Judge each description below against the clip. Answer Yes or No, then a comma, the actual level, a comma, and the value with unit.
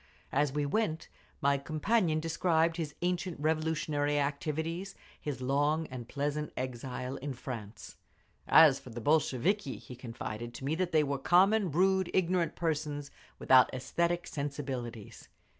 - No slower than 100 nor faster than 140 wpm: Yes, slow, 135 wpm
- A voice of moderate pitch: Yes, medium, 150 Hz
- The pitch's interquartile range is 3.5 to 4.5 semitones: Yes, average, 3.8 semitones